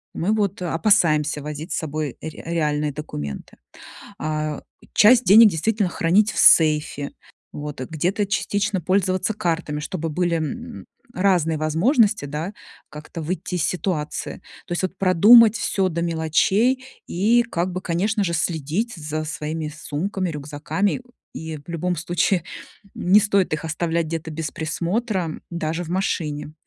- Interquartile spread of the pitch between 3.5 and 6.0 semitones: Yes, average, 4.1 semitones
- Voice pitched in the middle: Yes, medium, 170 Hz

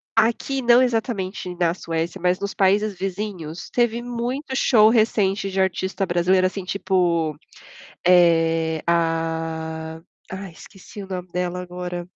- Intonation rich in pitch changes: No, average, 3.6 semitones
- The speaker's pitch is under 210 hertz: Yes, medium, 185 Hz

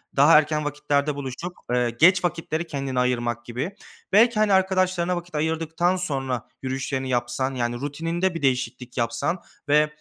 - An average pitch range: Yes, average, 4.9 semitones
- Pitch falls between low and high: Yes, medium, 150 Hz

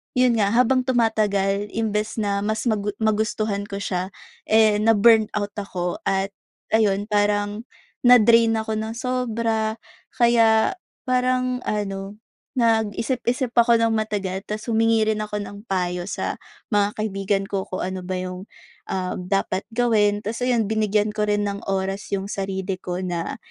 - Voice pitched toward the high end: Yes, high, 210 Hz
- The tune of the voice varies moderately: No, narrow, 2.3 semitones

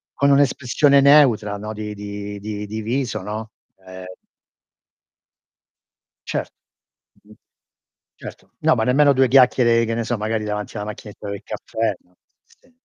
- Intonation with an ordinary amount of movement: Yes, average, 3.7 semitones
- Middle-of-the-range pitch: No, low, 110 Hz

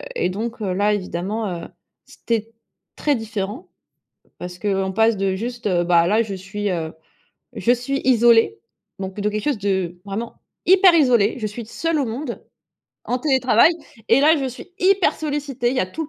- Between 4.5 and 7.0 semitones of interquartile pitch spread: Yes, average, 5.0 semitones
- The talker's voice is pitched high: Yes, high, 225 Hz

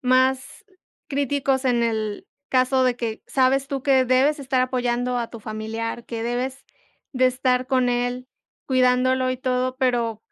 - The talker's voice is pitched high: Yes, very high, 255 Hz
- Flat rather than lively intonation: Yes, narrow, 1.3 semitones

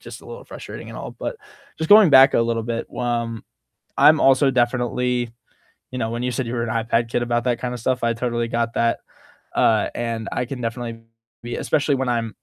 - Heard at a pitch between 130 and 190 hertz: No, low, 120 Hz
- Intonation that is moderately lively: No, narrow, 1.6 semitones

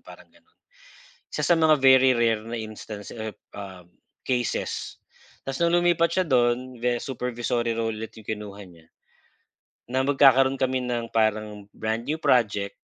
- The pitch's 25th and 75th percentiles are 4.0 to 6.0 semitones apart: No, average, 3.4 semitones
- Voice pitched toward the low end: Yes, low, 120 Hz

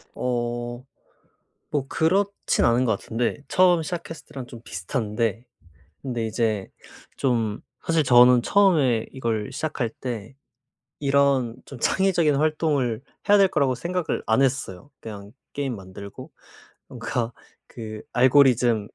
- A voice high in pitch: No, low, 125 Hz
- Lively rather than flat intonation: No, average, 4.3 semitones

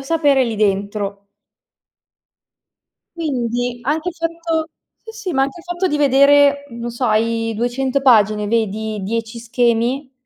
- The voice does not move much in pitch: No, average, 4.3 semitones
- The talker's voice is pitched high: Yes, high, 245 Hz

